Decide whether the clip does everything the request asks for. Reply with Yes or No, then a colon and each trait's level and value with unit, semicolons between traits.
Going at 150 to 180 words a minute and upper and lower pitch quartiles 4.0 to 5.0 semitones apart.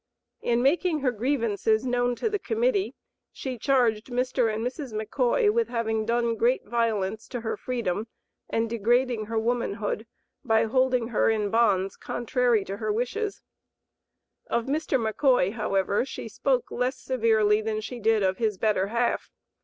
No: average, 155 wpm; average, 2.7 semitones